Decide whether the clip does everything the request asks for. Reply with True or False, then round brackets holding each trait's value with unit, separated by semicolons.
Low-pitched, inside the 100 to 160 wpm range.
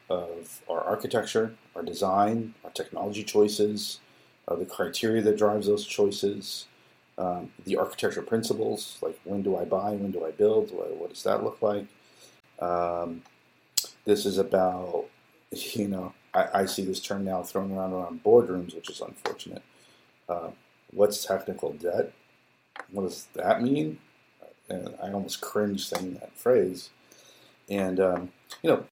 True (100 Hz; 150 wpm)